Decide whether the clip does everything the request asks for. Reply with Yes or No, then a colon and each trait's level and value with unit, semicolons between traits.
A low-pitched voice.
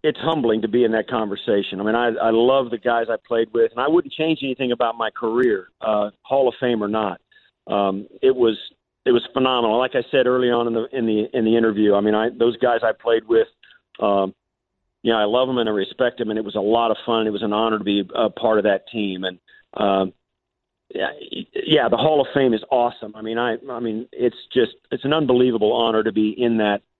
Yes: low, 115 Hz